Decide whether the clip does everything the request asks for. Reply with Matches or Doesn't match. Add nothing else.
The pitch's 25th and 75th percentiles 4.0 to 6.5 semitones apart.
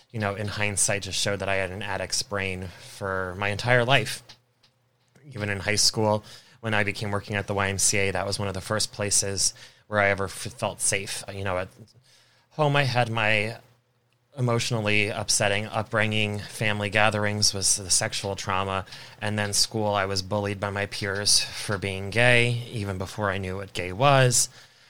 Doesn't match